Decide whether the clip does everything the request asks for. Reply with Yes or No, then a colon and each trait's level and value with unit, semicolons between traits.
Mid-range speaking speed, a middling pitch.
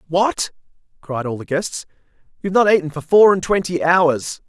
Yes: average, 190 wpm; medium, 175 Hz